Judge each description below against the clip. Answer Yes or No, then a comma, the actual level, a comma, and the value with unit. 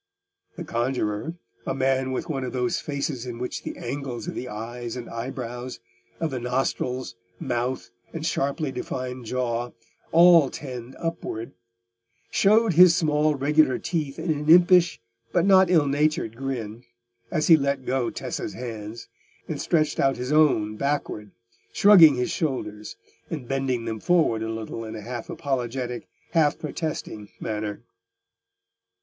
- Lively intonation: No, average, 4.7 semitones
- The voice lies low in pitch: Yes, low, 130 Hz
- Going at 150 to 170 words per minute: No, average, 140 wpm